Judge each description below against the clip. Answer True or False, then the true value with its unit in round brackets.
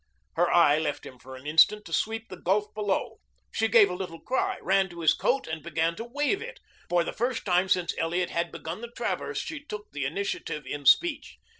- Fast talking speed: True (215 wpm)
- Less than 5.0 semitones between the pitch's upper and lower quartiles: False (5.3 semitones)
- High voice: False (180 Hz)